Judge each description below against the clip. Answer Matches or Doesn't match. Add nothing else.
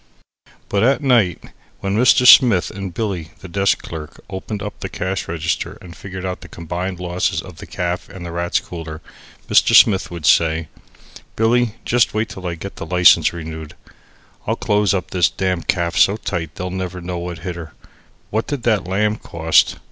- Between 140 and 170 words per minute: Doesn't match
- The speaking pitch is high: Doesn't match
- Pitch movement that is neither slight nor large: Matches